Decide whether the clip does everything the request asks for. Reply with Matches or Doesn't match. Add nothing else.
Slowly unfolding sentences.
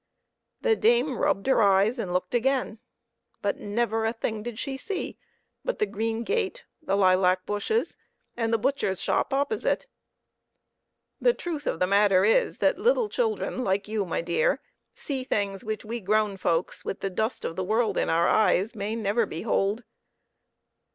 Doesn't match